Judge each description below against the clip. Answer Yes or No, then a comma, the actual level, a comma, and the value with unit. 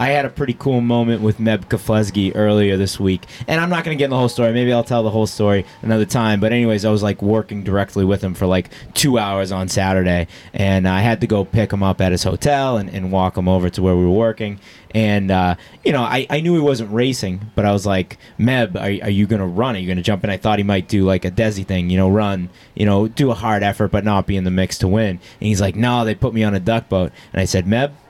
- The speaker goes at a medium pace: No, fast, 280 wpm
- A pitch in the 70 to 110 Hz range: Yes, low, 105 Hz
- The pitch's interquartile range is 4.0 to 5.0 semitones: No, average, 3.3 semitones